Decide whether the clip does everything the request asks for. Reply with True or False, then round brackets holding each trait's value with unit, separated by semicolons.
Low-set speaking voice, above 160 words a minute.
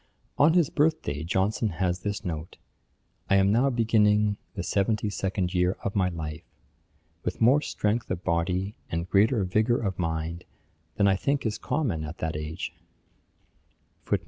False (95 Hz; 155 wpm)